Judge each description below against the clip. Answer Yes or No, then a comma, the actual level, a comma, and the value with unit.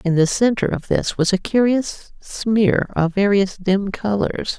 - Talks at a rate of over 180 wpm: No, average, 170 wpm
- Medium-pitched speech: No, high, 200 Hz